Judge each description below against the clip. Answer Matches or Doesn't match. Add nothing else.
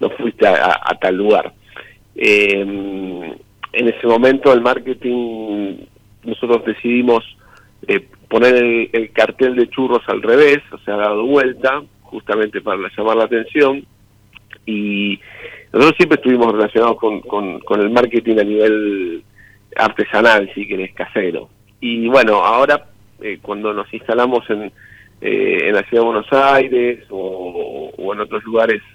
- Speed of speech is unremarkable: Matches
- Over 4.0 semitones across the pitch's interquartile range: Doesn't match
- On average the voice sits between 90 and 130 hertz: Matches